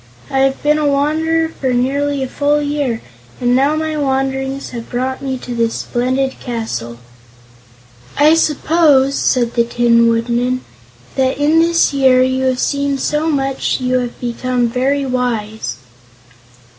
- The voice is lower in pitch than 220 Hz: No, very high, 265 Hz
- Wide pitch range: No, average, 2.7 semitones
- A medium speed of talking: Yes, average, 150 wpm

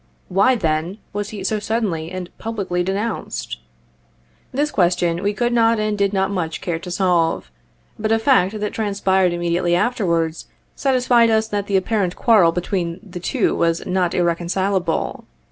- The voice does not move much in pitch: No, average, 3.7 semitones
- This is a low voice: No, high, 190 Hz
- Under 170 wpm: Yes, average, 155 wpm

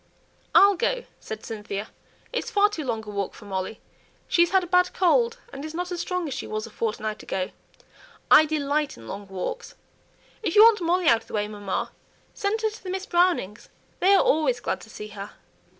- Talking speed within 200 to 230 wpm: Yes, fast, 205 wpm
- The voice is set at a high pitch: Yes, very high, 310 Hz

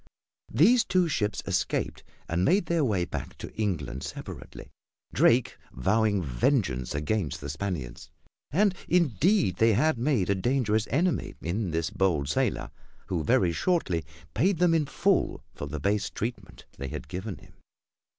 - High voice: No, low, 105 Hz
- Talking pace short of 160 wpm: Yes, average, 150 wpm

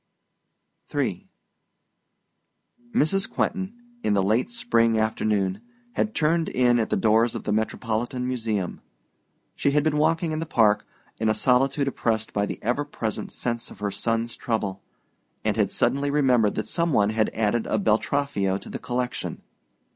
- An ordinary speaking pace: Yes, average, 155 wpm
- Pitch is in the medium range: No, low, 115 Hz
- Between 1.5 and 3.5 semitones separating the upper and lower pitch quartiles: No, average, 4.7 semitones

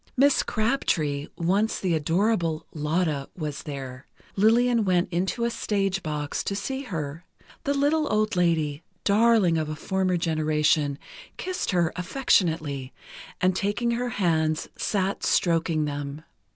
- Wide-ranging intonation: Yes, wide, 5.7 semitones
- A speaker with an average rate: No, slow, 130 wpm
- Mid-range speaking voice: Yes, medium, 175 Hz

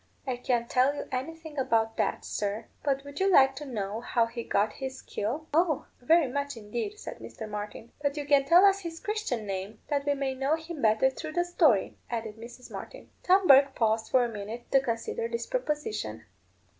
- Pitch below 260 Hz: No, very high, 265 Hz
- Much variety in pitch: No, average, 4.8 semitones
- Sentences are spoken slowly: No, average, 200 wpm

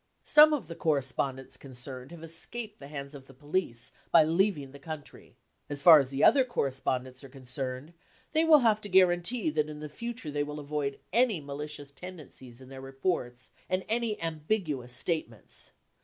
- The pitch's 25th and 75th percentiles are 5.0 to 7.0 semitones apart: Yes, wide, 5.5 semitones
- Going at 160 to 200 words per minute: Yes, average, 170 wpm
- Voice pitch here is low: No, medium, 150 Hz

